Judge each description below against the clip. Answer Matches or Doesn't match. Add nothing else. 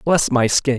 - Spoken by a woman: Doesn't match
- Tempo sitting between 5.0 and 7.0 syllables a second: Doesn't match